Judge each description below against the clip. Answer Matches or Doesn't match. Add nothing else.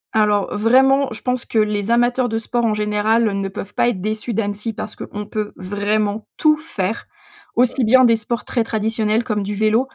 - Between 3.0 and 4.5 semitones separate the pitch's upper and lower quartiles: Doesn't match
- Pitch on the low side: Doesn't match